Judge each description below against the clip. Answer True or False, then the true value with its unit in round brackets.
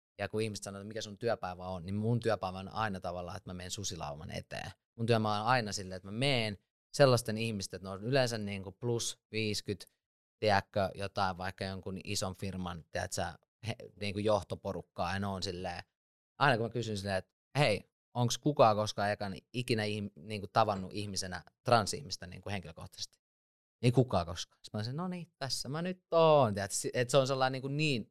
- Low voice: True (105 Hz)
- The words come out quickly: True (175 wpm)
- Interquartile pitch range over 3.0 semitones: True (3.7 semitones)